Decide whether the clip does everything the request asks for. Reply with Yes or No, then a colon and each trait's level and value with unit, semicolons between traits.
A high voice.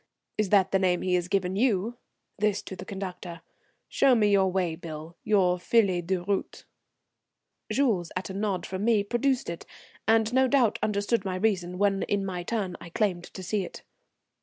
Yes: high, 195 Hz